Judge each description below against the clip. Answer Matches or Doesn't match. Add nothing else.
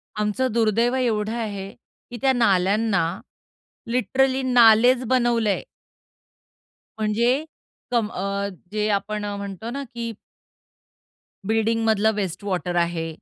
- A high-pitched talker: Matches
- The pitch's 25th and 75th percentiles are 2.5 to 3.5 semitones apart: Matches